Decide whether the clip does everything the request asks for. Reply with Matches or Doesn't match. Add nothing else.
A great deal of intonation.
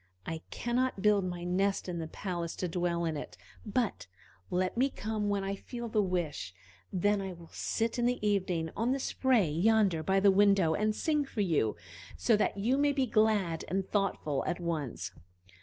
Doesn't match